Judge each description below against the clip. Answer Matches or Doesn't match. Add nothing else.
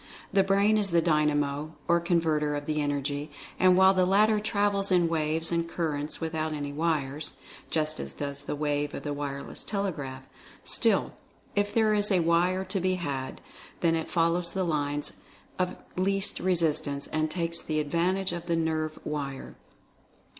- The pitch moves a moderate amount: Matches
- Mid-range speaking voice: Matches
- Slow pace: Doesn't match